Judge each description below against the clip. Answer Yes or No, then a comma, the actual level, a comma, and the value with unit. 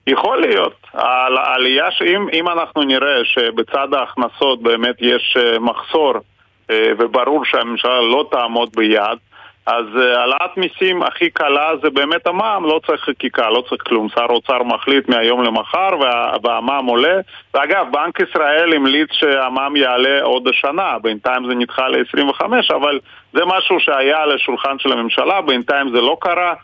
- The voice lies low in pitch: Yes, low, 130 Hz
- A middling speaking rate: Yes, average, 140 wpm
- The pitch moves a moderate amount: Yes, average, 4.4 semitones